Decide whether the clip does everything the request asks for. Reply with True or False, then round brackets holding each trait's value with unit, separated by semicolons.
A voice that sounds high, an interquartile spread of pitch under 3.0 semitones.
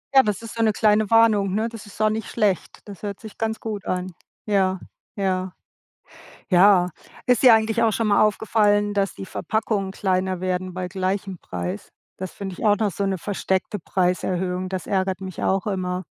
True (195 Hz; 2.4 semitones)